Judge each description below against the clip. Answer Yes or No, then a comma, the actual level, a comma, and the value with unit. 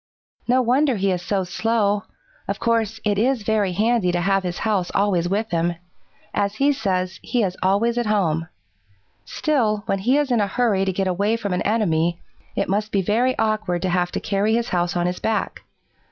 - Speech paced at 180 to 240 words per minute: Yes, average, 200 wpm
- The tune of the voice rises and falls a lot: No, average, 3.7 semitones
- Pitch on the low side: No, high, 205 Hz